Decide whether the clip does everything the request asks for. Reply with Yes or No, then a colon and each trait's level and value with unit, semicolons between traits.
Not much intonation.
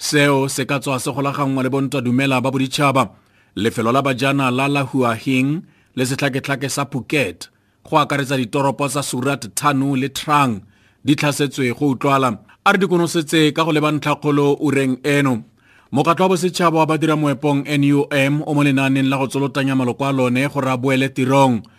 Yes: narrow, 1.8 semitones